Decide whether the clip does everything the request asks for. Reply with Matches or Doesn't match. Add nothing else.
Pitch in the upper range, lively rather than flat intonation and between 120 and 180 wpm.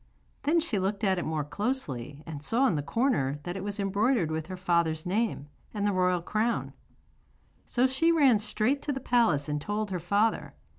Doesn't match